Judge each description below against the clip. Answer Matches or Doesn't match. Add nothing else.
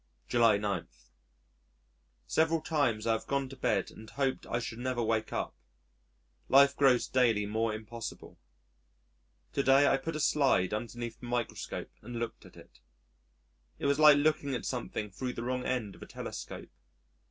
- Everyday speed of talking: Matches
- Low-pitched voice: Matches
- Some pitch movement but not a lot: Matches